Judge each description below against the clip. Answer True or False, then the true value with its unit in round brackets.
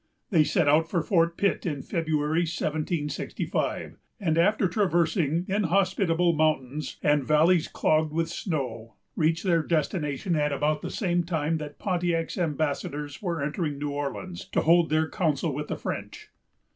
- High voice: False (160 Hz)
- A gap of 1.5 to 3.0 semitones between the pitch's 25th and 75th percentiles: True (2.7 semitones)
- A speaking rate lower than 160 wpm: True (145 wpm)